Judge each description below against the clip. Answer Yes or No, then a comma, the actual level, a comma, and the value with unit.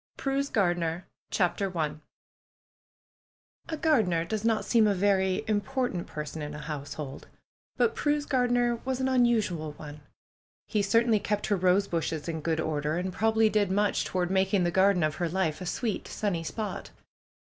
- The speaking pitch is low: No, high, 190 Hz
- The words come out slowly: No, average, 160 wpm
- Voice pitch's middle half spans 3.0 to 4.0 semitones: No, average, 5.2 semitones